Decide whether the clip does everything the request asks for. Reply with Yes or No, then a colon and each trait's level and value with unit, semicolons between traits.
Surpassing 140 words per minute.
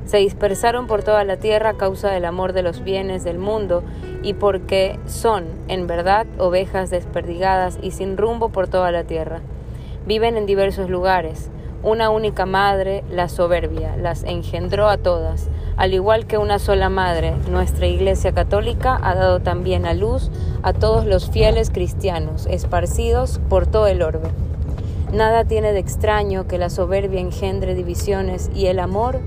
Yes: average, 160 wpm